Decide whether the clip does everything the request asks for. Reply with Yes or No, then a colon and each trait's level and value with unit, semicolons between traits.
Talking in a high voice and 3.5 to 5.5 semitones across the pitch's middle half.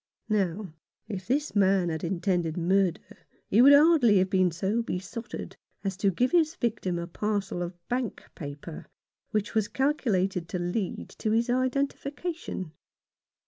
Yes: high, 195 Hz; average, 5.1 semitones